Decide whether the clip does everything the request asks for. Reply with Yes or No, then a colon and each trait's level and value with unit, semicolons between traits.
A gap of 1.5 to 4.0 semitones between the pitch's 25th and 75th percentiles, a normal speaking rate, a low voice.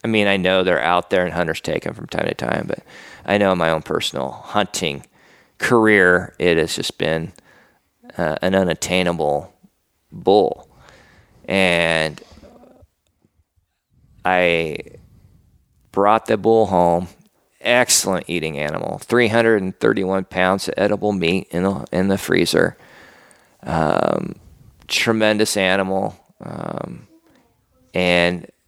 No: narrow, 2.6 semitones; slow, 125 wpm; very low, 90 Hz